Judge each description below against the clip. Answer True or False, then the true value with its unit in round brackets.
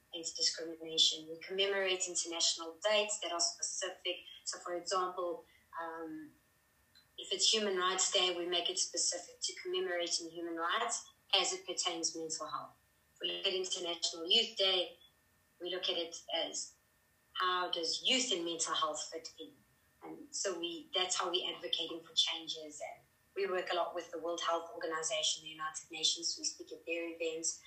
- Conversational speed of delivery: True (165 wpm)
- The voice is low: False (170 Hz)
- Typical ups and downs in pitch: False (2.2 semitones)